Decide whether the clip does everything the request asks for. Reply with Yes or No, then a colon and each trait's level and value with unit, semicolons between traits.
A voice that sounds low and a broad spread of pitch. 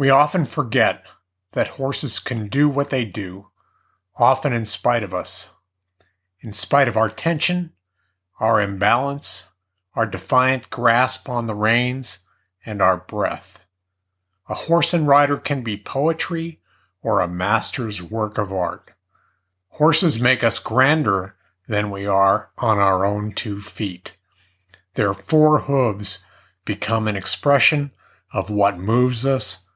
Yes: low, 110 Hz; wide, 6.0 semitones